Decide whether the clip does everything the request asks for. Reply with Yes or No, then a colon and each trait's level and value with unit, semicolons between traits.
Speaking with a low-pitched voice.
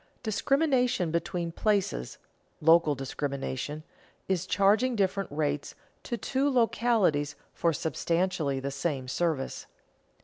No: medium, 170 Hz